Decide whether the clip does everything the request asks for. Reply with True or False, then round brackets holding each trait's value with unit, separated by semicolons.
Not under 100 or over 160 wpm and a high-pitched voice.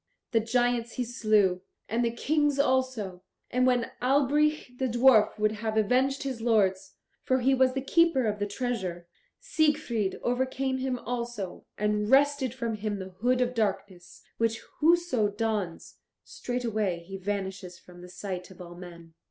True (155 wpm; 230 Hz)